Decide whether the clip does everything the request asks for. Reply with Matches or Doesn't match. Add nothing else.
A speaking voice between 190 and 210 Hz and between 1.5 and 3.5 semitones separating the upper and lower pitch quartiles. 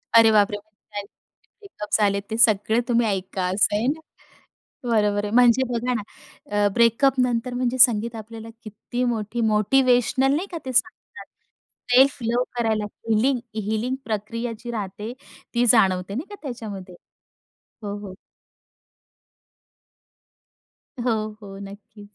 Doesn't match